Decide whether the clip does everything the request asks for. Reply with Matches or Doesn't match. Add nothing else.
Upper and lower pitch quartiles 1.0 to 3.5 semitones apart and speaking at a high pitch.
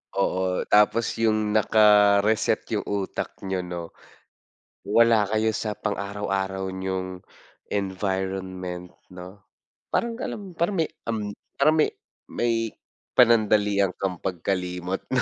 Doesn't match